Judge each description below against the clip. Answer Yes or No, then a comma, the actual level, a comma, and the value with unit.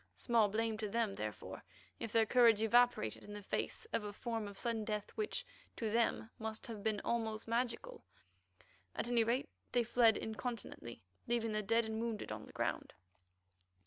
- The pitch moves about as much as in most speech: No, narrow, 1.7 semitones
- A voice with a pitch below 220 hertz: No, high, 225 Hz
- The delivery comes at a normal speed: Yes, average, 170 wpm